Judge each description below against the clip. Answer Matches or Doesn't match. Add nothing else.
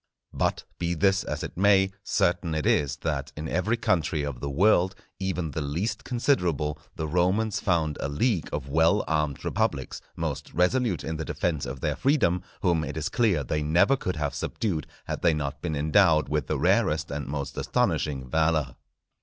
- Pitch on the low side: Matches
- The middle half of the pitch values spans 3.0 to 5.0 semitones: Matches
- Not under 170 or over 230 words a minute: Matches